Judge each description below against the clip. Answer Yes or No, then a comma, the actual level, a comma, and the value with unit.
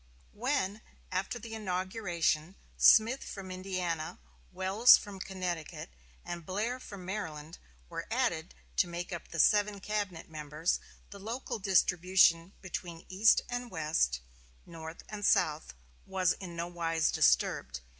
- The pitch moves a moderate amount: Yes, average, 3.6 semitones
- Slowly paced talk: Yes, slow, 125 wpm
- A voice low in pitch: No, medium, 185 Hz